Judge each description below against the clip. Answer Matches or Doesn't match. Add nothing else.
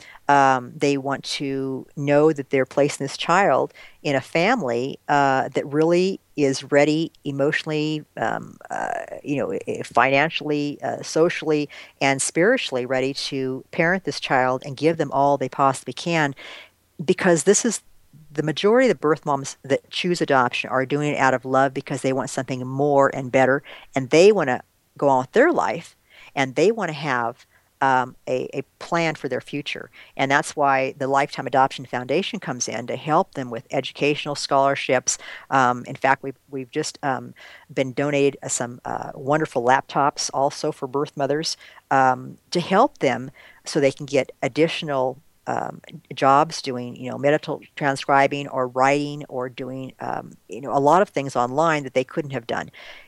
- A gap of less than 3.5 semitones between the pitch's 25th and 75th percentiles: Matches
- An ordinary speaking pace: Matches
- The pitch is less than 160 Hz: Matches